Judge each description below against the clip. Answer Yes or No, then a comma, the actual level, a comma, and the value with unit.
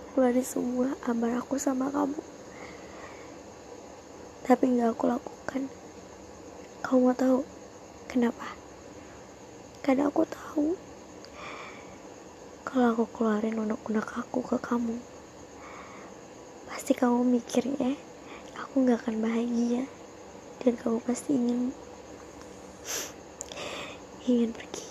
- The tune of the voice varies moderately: No, narrow, 2.2 semitones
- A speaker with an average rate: Yes, average, 95 wpm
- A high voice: Yes, very high, 250 Hz